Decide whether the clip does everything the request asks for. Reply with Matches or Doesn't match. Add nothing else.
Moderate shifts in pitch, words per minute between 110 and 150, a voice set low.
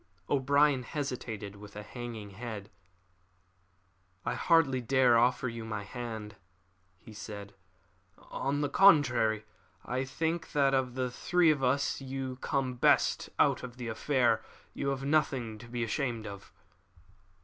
Matches